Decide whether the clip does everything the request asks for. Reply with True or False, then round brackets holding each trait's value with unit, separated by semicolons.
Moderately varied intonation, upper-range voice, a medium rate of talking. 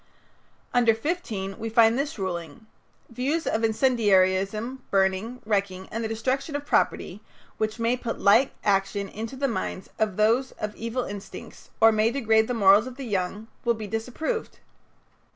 True (3.6 semitones; 225 Hz; 155 wpm)